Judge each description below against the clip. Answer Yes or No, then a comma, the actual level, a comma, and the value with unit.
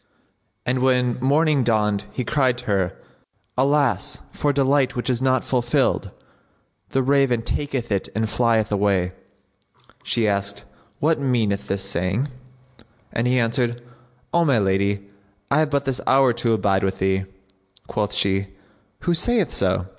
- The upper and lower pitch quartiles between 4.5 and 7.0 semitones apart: Yes, average, 5.0 semitones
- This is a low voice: Yes, low, 120 Hz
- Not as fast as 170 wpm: Yes, average, 145 wpm